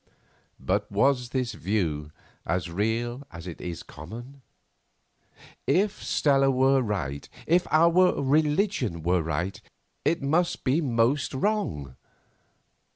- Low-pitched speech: Yes, low, 120 Hz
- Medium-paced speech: No, slow, 110 wpm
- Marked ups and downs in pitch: Yes, wide, 8.3 semitones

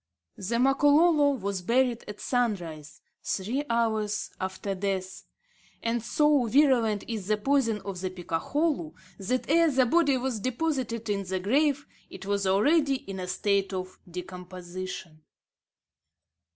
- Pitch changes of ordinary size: No, wide, 6.0 semitones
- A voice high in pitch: Yes, high, 215 Hz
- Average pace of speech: No, slow, 130 wpm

